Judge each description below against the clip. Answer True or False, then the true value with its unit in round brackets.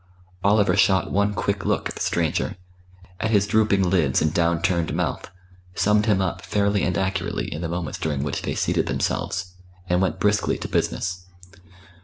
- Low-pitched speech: True (95 Hz)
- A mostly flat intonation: False (3.0 semitones)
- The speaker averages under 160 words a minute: False (175 wpm)